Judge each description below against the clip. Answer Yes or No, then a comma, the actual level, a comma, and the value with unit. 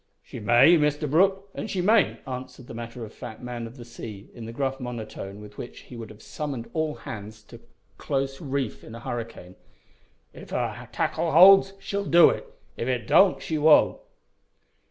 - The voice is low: Yes, low, 130 Hz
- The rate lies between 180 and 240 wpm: Yes, average, 185 wpm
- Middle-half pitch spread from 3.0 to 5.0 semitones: No, wide, 5.4 semitones